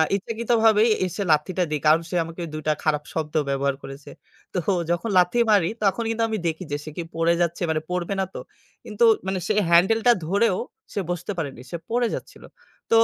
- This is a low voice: No, medium, 180 Hz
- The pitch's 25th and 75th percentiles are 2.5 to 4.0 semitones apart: No, average, 5.0 semitones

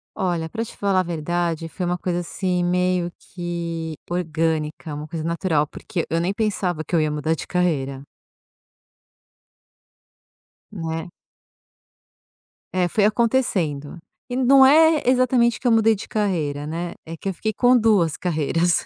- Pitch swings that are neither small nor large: Yes, average, 4.2 semitones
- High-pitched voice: No, medium, 175 Hz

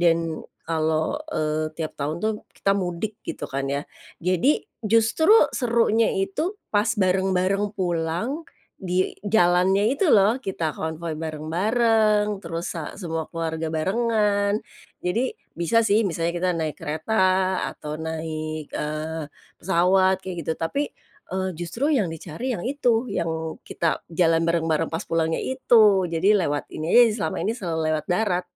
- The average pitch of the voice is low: No, medium, 175 Hz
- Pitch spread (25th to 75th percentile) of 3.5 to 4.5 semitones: Yes, average, 4.1 semitones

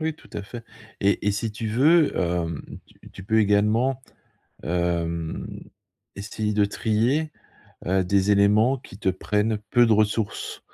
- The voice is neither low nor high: No, low, 105 Hz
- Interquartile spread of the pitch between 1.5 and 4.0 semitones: Yes, average, 3.0 semitones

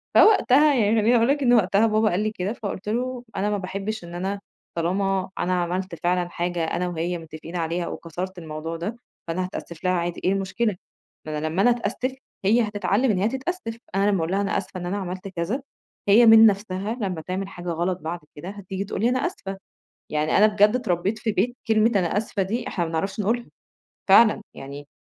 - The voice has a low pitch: No, high, 195 Hz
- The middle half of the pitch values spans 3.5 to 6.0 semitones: Yes, average, 3.8 semitones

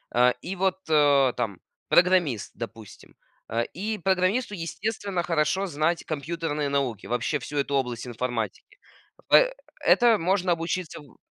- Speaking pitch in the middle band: Yes, medium, 160 Hz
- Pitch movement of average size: No, wide, 6.4 semitones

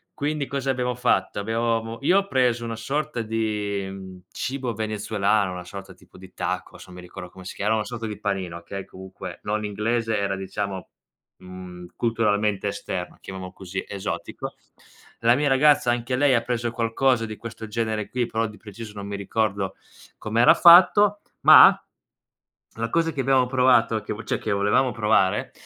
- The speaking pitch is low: Yes, low, 110 Hz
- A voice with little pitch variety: No, average, 3.6 semitones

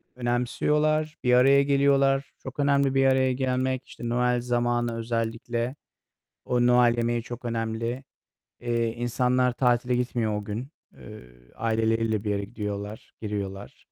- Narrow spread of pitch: Yes, narrow, 2.3 semitones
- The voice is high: No, low, 120 Hz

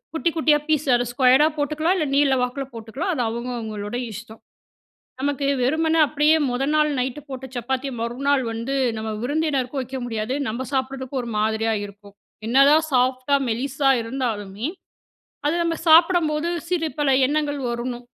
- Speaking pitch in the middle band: No, very high, 265 Hz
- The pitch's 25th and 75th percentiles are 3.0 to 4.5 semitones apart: Yes, average, 3.9 semitones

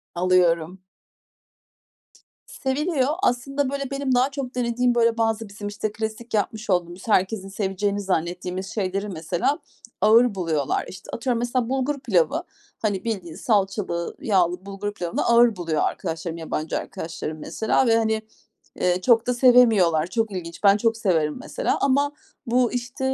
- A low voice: No, high, 215 Hz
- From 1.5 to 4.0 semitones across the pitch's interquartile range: No, average, 5.1 semitones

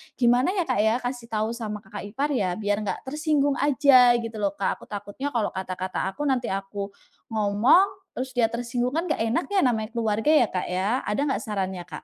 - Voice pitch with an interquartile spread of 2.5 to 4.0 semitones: No, average, 4.5 semitones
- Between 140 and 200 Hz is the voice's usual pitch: No, high, 235 Hz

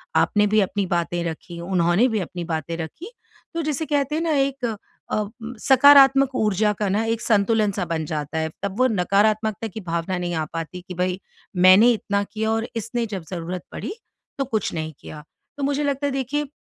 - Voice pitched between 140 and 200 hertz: No, high, 210 Hz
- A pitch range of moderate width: No, wide, 6.6 semitones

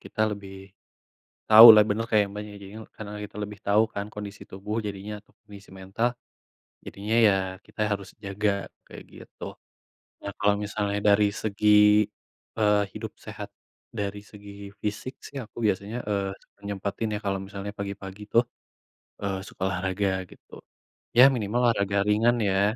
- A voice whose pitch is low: Yes, low, 105 Hz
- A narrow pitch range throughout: Yes, narrow, 1.2 semitones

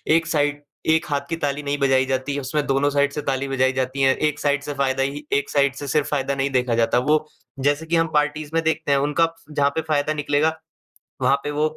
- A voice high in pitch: No, medium, 145 Hz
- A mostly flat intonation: Yes, narrow, 1.7 semitones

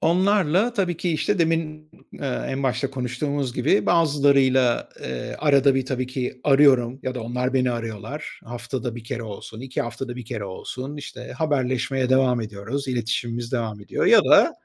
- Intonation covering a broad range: No, average, 3.2 semitones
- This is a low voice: Yes, low, 130 Hz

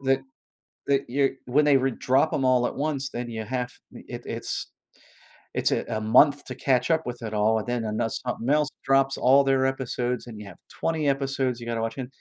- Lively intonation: No, narrow, 2.5 semitones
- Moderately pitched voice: No, low, 130 Hz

